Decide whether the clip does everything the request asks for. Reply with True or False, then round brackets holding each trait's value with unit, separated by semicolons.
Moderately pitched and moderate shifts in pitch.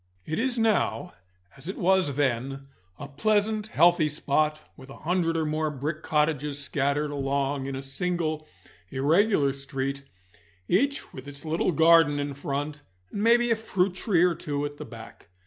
True (150 Hz; 4.2 semitones)